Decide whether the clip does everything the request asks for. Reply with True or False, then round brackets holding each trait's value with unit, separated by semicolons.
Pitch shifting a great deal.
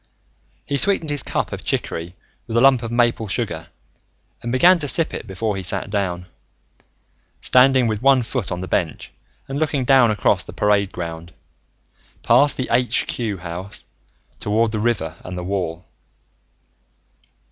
True (5.9 semitones)